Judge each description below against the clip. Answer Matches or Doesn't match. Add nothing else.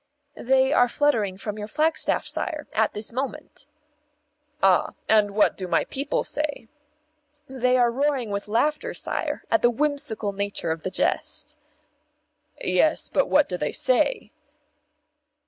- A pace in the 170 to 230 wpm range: Doesn't match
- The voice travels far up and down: Matches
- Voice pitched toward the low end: Doesn't match